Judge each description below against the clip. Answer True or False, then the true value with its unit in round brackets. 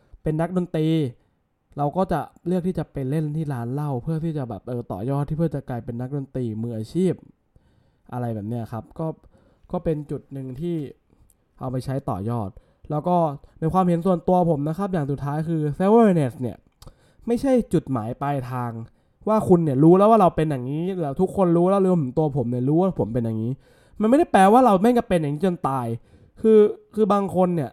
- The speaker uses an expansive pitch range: True (6.2 semitones)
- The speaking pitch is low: False (155 Hz)